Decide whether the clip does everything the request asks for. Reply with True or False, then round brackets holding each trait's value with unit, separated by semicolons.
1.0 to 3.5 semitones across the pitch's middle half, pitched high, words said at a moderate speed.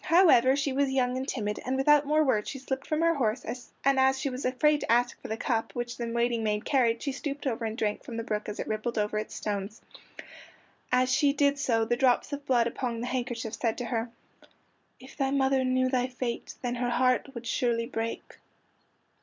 False (2.6 semitones; 250 Hz; 220 wpm)